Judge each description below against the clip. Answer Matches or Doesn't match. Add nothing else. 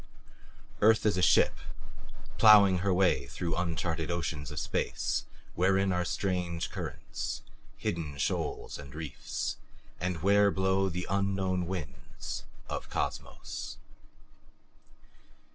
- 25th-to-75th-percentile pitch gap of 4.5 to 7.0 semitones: Doesn't match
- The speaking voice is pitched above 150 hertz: Doesn't match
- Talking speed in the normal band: Doesn't match